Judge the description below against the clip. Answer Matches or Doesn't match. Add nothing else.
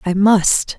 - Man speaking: Doesn't match